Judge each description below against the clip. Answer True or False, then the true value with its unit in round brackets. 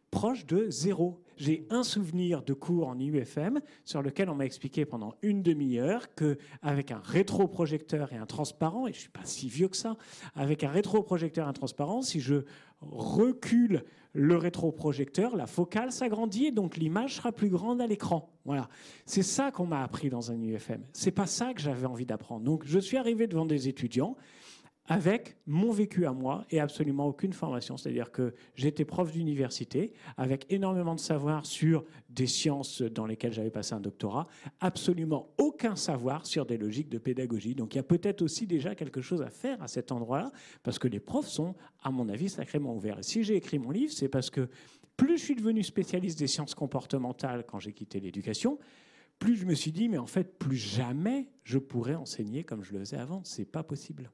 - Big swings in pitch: True (6.4 semitones)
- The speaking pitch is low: False (155 Hz)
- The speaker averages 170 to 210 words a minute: True (200 wpm)